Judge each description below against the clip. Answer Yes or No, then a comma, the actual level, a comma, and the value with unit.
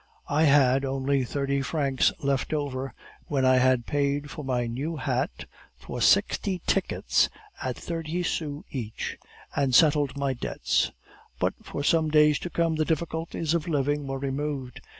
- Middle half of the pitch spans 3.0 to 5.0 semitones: No, narrow, 2.6 semitones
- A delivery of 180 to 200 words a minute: No, average, 150 wpm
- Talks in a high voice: No, medium, 140 Hz